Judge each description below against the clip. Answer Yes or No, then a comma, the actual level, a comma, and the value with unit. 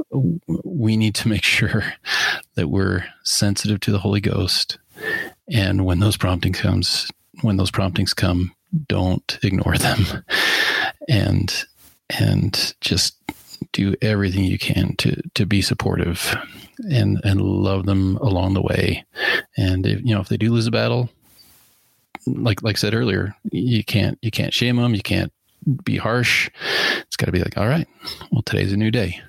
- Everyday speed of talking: Yes, average, 160 wpm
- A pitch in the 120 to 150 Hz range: No, low, 105 Hz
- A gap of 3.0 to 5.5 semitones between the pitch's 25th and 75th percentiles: Yes, average, 3.4 semitones